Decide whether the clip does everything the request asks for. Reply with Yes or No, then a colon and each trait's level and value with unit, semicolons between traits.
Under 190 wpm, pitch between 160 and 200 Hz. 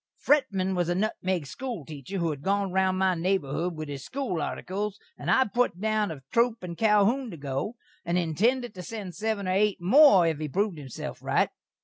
No: average, 200 wpm; high, 190 Hz